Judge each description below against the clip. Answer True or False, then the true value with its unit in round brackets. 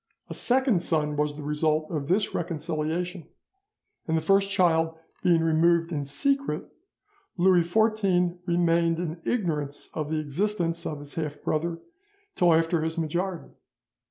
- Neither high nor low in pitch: True (165 Hz)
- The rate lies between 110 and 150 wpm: True (140 wpm)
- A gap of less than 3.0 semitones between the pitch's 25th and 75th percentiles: True (2.4 semitones)